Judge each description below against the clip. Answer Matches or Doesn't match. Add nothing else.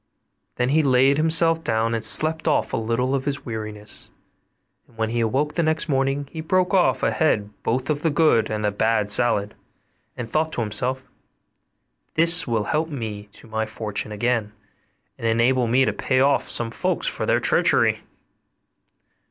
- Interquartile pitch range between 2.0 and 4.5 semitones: Doesn't match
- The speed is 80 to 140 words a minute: Doesn't match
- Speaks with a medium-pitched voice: Doesn't match